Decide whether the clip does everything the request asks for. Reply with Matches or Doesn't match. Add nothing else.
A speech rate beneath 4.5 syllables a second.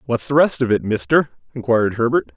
Doesn't match